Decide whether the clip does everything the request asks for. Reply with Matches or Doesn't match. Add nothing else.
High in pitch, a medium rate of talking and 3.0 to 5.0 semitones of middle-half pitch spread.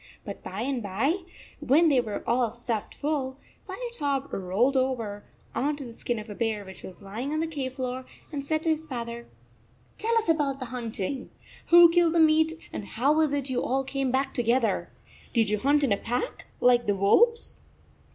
Matches